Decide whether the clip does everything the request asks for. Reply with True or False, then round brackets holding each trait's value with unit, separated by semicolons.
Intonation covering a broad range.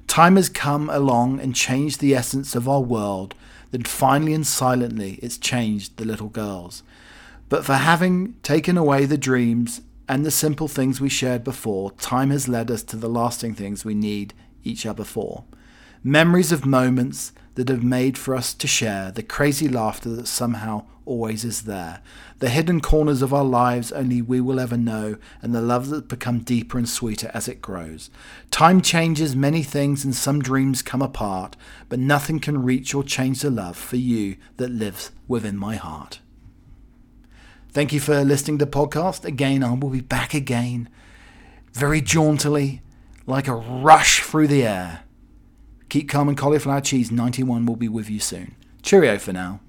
False (3.7 semitones)